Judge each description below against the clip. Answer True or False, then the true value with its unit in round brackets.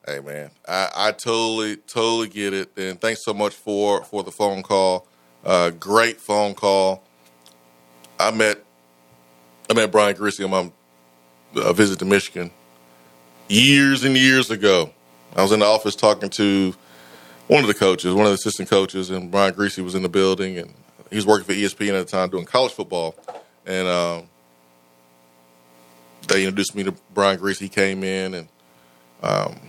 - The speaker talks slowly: False (170 wpm)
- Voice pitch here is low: True (95 Hz)